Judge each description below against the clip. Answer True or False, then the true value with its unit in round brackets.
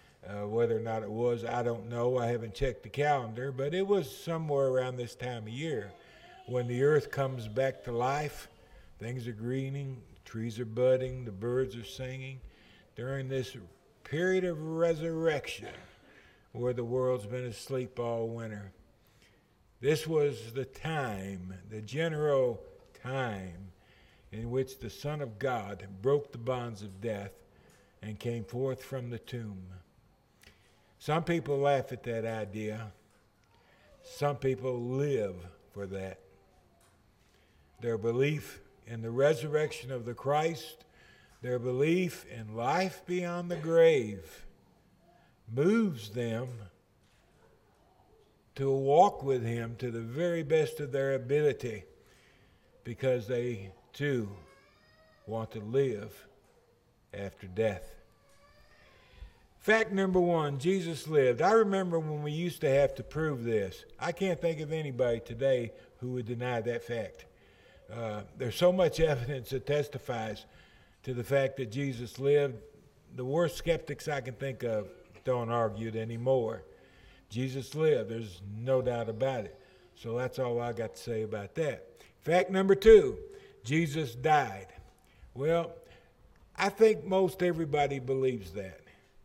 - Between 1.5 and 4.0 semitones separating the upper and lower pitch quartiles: False (4.5 semitones)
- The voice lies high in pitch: False (125 Hz)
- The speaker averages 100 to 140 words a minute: True (135 wpm)